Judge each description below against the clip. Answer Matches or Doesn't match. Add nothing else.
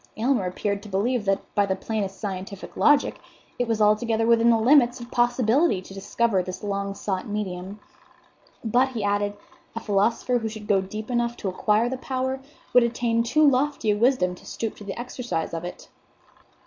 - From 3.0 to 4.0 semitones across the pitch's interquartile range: Matches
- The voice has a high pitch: Matches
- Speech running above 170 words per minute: Matches